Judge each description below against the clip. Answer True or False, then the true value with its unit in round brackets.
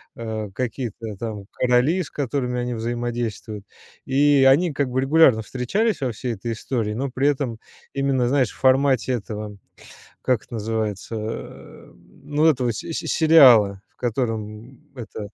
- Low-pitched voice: True (125 Hz)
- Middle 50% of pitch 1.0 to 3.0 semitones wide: False (3.6 semitones)